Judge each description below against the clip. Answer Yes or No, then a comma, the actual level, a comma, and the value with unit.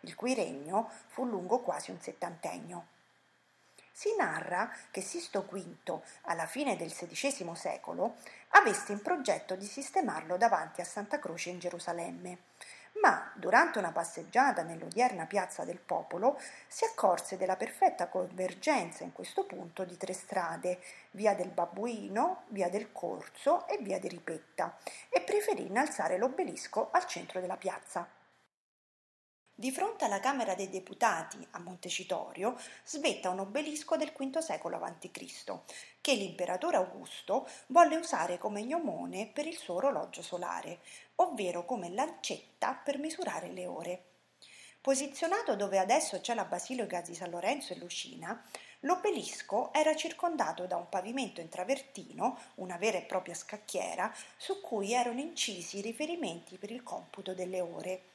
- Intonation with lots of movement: Yes, wide, 8.4 semitones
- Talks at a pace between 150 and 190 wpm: No, average, 140 wpm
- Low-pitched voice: No, high, 215 Hz